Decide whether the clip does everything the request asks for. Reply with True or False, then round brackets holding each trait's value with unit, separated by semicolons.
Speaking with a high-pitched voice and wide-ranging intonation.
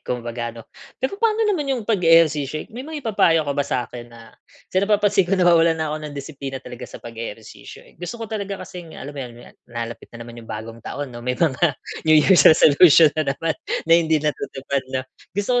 False (155 Hz; 6.8 semitones)